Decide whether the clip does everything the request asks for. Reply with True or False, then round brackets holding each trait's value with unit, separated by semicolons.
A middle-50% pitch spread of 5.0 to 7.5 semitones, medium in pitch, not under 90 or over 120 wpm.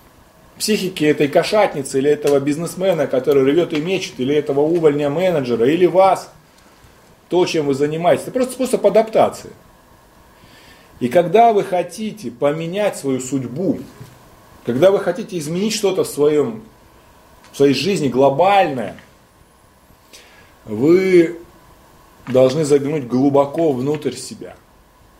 True (5.3 semitones; 155 Hz; 110 wpm)